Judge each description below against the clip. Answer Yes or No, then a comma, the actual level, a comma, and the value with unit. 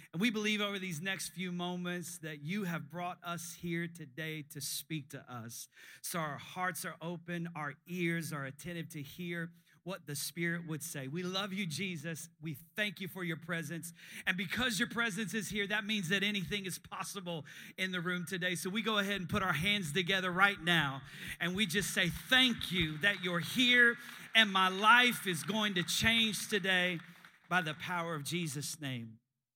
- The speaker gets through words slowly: No, average, 195 wpm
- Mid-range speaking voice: Yes, medium, 175 Hz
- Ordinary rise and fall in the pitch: Yes, average, 3.6 semitones